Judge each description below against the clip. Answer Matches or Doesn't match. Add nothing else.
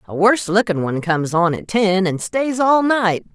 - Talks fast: Matches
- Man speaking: Doesn't match